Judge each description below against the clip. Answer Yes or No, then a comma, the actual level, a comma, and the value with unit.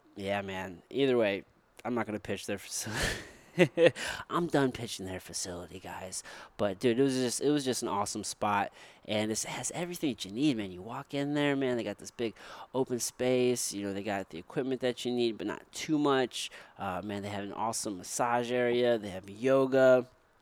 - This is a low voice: Yes, low, 120 Hz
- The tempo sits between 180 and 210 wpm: Yes, fast, 205 wpm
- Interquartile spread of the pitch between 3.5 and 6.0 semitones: Yes, average, 4.5 semitones